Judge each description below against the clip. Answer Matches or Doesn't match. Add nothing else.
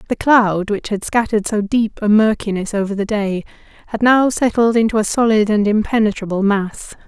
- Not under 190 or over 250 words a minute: Doesn't match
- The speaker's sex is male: Doesn't match